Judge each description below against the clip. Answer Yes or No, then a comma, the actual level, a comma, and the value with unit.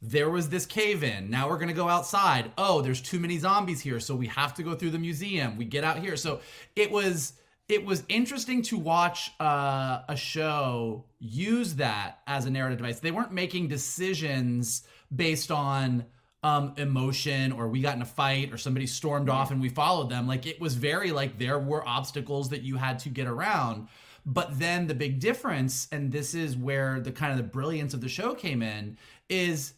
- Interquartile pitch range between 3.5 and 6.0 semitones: Yes, average, 4.6 semitones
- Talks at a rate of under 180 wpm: No, fast, 205 wpm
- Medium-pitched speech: Yes, medium, 145 Hz